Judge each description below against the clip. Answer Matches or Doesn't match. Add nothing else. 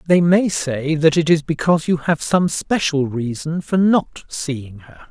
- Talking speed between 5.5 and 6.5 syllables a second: Doesn't match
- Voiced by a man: Matches